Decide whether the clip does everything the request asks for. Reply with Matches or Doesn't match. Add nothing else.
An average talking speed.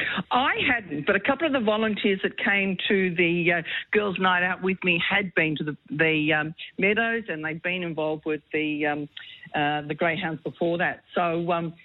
Doesn't match